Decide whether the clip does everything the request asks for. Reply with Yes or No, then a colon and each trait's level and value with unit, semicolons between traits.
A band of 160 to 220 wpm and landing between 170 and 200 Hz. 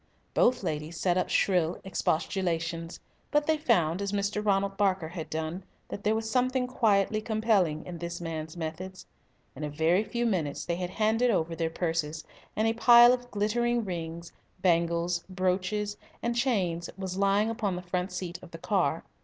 Yes: average, 170 wpm; medium, 185 Hz